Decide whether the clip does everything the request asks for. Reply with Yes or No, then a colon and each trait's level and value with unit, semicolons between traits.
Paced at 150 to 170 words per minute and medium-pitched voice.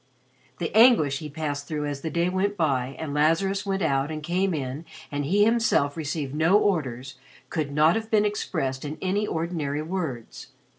No: average, 180 wpm; medium, 155 Hz